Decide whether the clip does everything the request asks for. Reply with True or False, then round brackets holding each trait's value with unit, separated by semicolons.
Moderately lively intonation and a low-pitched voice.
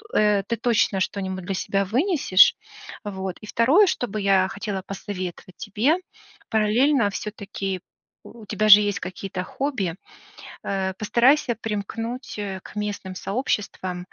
False (3.3 semitones; 205 Hz)